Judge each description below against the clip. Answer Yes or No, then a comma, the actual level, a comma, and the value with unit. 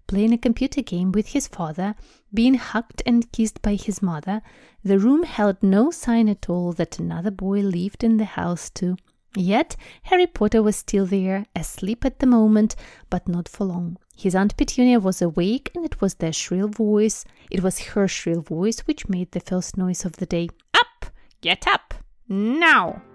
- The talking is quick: Yes, fast, 185 wpm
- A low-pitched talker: No, high, 205 Hz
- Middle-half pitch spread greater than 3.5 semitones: Yes, average, 4.0 semitones